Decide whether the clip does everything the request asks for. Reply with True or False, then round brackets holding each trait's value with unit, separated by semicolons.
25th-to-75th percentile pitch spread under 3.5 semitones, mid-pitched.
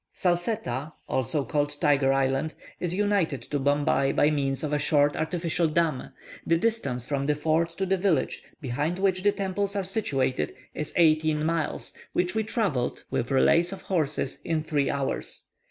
False (4.1 semitones; 155 Hz)